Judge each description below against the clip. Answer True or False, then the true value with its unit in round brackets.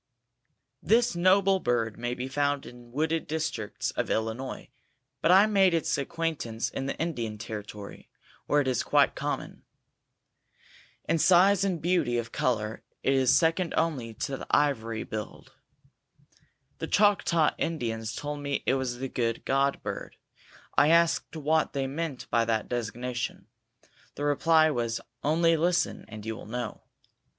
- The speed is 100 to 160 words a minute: True (145 wpm)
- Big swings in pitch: True (5.8 semitones)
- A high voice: False (140 Hz)